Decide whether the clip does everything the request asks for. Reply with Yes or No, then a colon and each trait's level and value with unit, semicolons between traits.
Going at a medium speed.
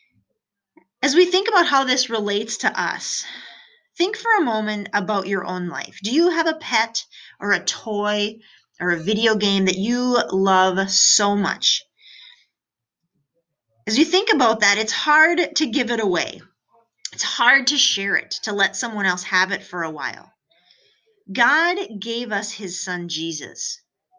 Yes: average, 160 wpm